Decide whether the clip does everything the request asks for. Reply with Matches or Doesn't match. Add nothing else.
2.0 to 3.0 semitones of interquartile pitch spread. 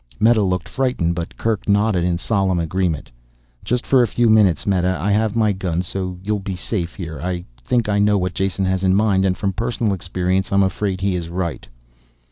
Matches